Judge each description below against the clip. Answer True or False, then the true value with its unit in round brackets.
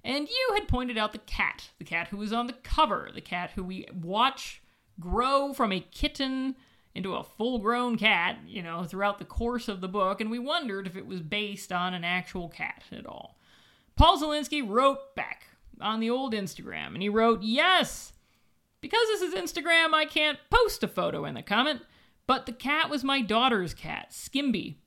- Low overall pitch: False (235 Hz)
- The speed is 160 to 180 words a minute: False (195 wpm)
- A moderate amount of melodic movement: False (6.6 semitones)